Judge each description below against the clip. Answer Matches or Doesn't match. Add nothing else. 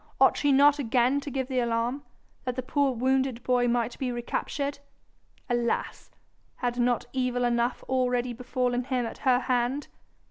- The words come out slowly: Doesn't match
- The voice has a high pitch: Matches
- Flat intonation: Matches